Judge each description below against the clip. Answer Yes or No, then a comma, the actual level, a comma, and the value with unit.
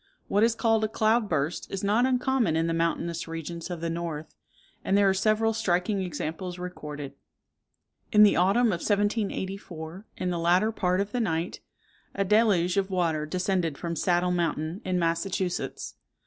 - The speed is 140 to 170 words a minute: Yes, average, 165 wpm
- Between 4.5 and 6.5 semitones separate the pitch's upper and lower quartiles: No, average, 3.6 semitones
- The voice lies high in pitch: No, medium, 180 Hz